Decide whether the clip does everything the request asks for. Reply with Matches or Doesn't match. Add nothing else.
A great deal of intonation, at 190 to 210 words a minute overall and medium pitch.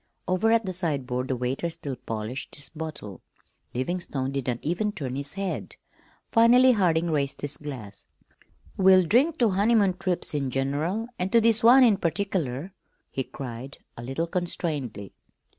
Doesn't match